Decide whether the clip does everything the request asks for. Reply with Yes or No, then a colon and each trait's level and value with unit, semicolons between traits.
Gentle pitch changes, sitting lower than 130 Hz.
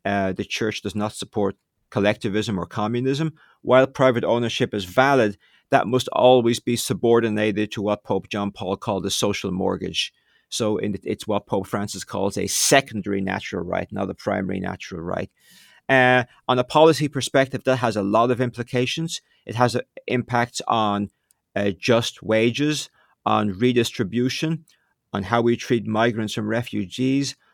No: average, 3.7 semitones; low, 115 Hz